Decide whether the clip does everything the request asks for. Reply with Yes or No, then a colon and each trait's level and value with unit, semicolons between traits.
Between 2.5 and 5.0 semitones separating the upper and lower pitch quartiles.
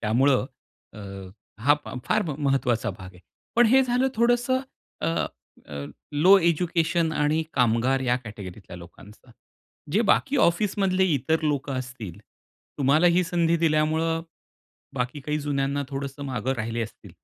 No: wide, 5.4 semitones